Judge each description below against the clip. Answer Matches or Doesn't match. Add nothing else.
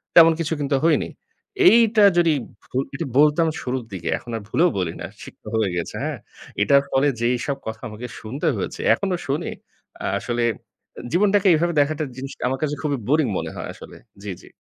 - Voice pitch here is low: Doesn't match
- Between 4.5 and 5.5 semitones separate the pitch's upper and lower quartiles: Matches